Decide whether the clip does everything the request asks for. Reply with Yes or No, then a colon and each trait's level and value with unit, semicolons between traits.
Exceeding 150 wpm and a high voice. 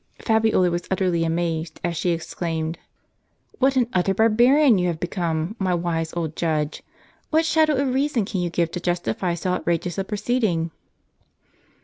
No: average, 165 wpm; medium, 180 Hz